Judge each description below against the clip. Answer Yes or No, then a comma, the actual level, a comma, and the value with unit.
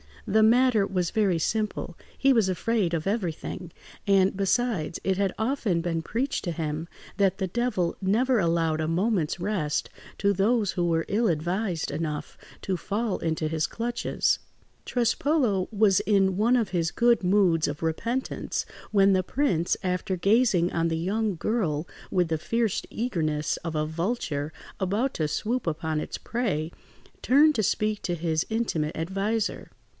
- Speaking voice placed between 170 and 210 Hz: Yes, high, 190 Hz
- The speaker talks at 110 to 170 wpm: Yes, average, 155 wpm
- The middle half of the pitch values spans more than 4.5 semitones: Yes, average, 5.1 semitones